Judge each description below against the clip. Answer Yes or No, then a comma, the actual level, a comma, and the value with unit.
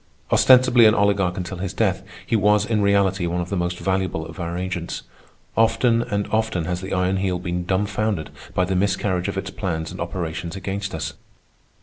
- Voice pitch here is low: Yes, very low, 95 Hz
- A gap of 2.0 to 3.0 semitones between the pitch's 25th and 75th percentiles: Yes, narrow, 2.6 semitones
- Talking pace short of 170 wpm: No, average, 190 wpm